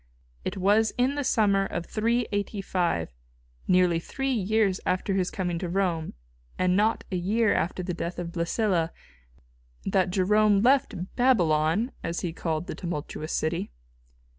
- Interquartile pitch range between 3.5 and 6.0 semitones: Yes, average, 4.0 semitones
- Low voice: No, medium, 185 Hz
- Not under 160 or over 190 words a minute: No, average, 140 wpm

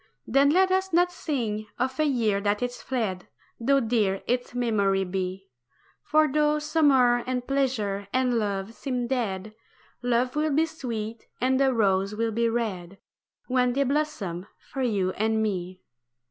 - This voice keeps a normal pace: Yes, average, 155 wpm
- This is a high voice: Yes, high, 240 Hz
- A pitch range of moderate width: Yes, average, 4.9 semitones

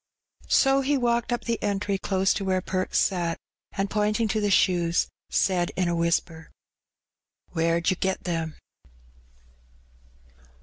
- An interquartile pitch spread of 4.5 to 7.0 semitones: No, average, 3.5 semitones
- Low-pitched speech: No, high, 190 Hz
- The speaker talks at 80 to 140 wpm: Yes, slow, 135 wpm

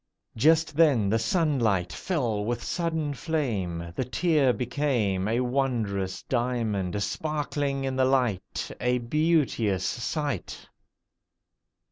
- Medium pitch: No, low, 125 Hz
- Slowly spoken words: Yes, slow, 105 wpm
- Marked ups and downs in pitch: Yes, wide, 5.9 semitones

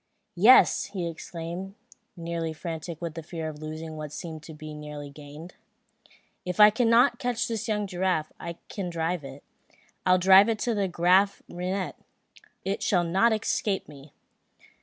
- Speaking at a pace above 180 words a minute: No, average, 150 wpm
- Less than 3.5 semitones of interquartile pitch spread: No, average, 3.9 semitones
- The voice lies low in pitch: No, medium, 175 Hz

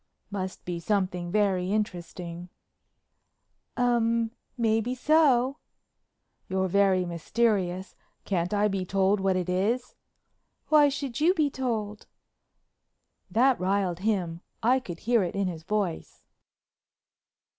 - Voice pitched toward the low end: No, high, 200 Hz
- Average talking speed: No, slow, 105 wpm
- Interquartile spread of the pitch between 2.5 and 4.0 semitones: No, average, 4.5 semitones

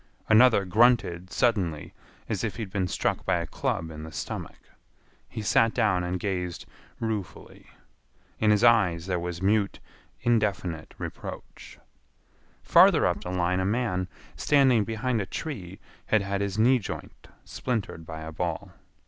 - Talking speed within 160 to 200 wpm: No, average, 150 wpm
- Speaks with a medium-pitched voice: No, low, 100 Hz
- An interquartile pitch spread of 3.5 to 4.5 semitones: Yes, average, 4.0 semitones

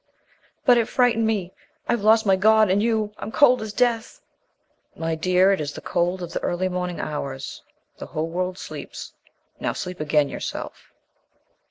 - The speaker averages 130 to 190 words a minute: Yes, average, 170 wpm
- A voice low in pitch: No, high, 190 Hz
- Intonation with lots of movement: No, average, 4.1 semitones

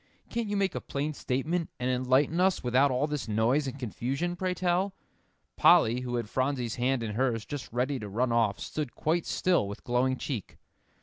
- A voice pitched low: Yes, low, 130 Hz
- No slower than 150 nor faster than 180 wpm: No, average, 190 wpm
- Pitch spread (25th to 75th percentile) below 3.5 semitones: No, average, 4.2 semitones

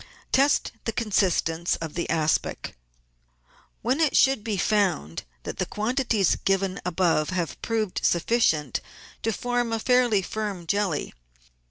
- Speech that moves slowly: Yes, slow, 130 wpm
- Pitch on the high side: Yes, high, 200 Hz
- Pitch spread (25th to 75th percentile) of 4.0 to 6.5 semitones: Yes, average, 5.1 semitones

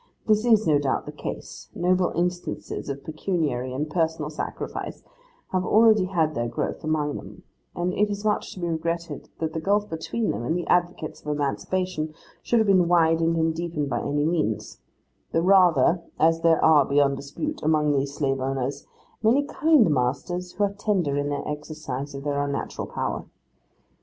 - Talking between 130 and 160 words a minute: No, average, 175 wpm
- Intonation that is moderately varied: Yes, average, 4.1 semitones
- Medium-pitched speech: Yes, medium, 160 Hz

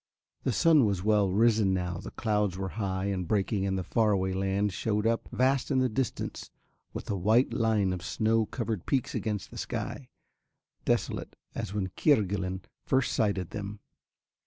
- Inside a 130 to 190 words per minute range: Yes, average, 170 wpm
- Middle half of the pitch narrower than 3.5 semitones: Yes, average, 3.0 semitones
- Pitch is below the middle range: Yes, low, 105 Hz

